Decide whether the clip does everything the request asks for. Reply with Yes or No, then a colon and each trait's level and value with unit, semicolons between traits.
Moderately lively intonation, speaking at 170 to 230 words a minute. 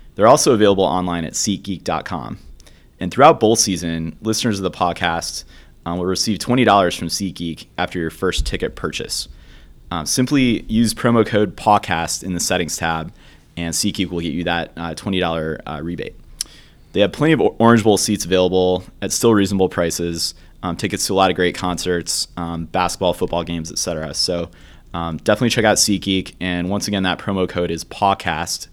Yes: average, 3.2 semitones; average, 180 wpm